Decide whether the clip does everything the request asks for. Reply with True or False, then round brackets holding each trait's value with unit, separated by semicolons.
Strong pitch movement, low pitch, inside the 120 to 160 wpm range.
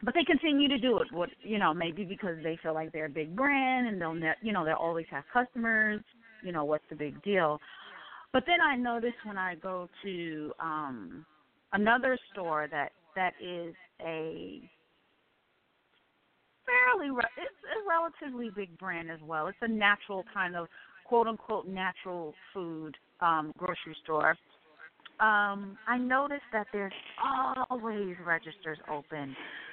False (6.3 semitones; 190 Hz; 155 wpm)